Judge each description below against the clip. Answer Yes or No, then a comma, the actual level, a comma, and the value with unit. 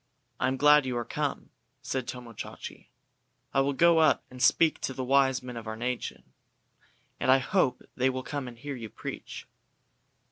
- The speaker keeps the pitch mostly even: Yes, narrow, 2.0 semitones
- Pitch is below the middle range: Yes, low, 130 Hz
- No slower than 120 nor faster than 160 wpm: No, average, 185 wpm